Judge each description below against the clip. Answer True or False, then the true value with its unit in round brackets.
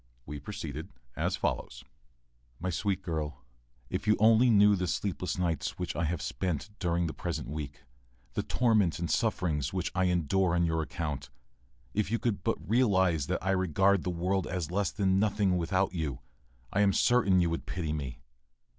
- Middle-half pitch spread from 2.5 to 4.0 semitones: True (3.4 semitones)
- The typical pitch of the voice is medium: False (90 Hz)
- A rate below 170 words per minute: False (175 wpm)